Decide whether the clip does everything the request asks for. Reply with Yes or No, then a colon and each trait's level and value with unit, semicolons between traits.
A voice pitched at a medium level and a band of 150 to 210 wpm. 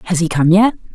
No: medium, 180 Hz; fast, 255 wpm